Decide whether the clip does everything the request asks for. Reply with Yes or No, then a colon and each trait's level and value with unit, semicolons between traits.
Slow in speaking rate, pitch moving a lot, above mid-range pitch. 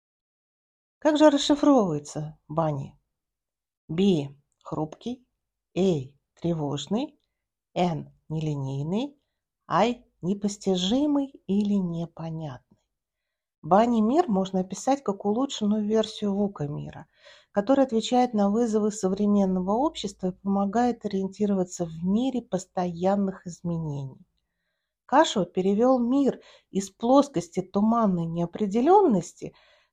Yes: slow, 85 wpm; wide, 5.7 semitones; high, 195 Hz